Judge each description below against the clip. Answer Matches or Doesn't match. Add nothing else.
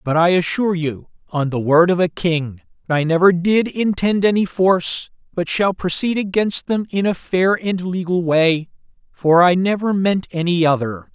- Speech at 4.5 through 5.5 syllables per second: Matches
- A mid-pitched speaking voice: Matches